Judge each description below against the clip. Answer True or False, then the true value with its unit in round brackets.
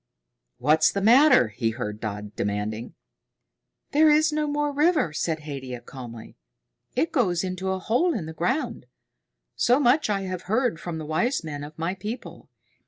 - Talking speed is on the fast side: False (165 wpm)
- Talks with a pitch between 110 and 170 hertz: False (185 Hz)